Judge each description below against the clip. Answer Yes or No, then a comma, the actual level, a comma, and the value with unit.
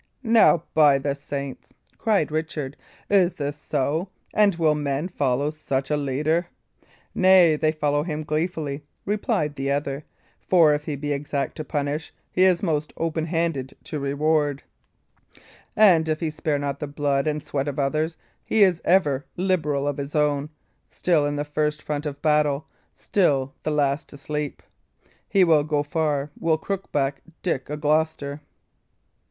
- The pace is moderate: Yes, average, 160 wpm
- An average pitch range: No, narrow, 2.1 semitones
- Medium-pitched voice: Yes, medium, 150 Hz